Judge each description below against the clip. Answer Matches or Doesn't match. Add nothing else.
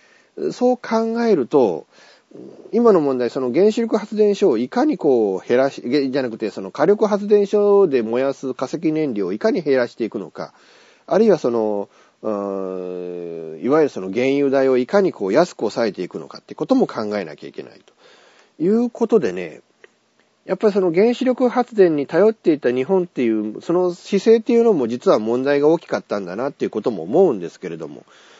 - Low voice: Doesn't match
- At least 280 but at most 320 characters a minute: Doesn't match